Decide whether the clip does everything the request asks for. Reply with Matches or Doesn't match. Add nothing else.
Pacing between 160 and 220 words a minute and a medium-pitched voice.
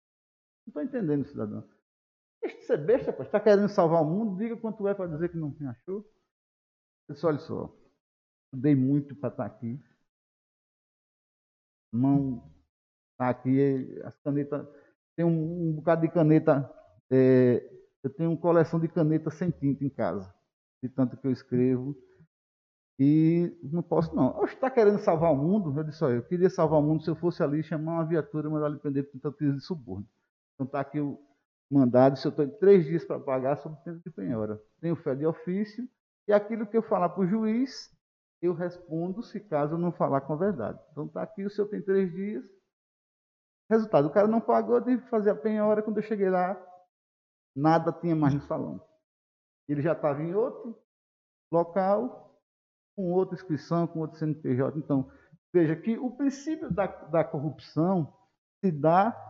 Matches